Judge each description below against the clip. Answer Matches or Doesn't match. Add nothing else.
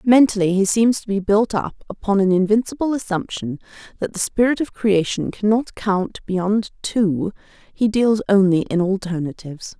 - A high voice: Matches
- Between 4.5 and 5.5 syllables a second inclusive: Matches